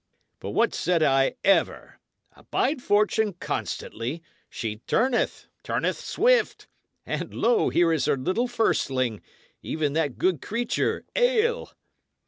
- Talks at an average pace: No, slow, 115 wpm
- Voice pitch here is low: No, medium, 185 Hz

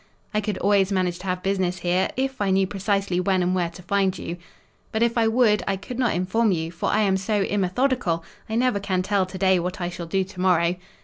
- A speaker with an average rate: No, fast, 240 wpm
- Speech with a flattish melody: Yes, narrow, 2.3 semitones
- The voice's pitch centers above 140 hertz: Yes, high, 190 Hz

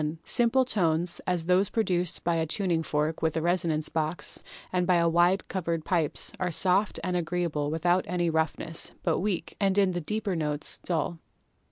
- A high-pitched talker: No, medium, 175 Hz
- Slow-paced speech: No, average, 170 wpm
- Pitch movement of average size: No, narrow, 2.2 semitones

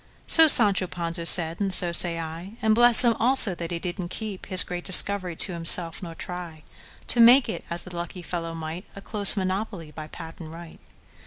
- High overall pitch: No, medium, 180 Hz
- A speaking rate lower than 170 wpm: No, average, 175 wpm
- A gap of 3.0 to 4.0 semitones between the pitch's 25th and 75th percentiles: Yes, average, 3.3 semitones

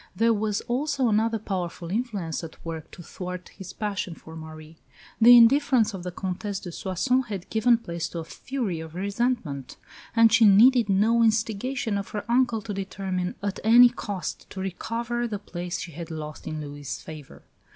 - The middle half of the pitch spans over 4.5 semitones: Yes, average, 4.9 semitones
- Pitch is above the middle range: Yes, high, 200 Hz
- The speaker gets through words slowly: No, average, 175 wpm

